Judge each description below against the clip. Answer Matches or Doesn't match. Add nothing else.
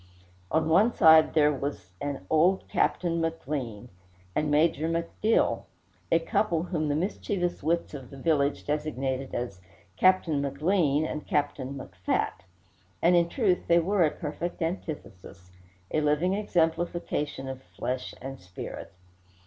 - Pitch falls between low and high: Matches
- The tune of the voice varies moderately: Matches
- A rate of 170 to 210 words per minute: Doesn't match